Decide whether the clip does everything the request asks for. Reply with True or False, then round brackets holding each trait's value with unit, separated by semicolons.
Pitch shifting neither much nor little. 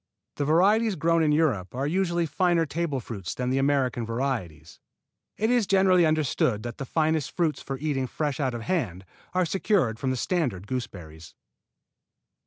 False (6.1 semitones)